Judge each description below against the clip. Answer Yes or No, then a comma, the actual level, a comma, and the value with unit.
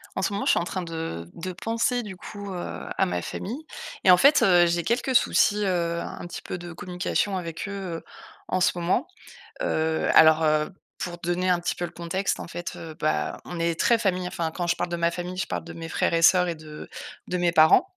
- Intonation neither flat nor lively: No, narrow, 2.2 semitones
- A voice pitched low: No, medium, 175 Hz